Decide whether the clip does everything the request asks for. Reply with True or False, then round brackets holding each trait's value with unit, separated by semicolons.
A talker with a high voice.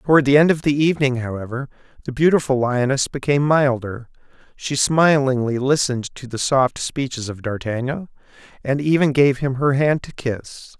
False (135 Hz)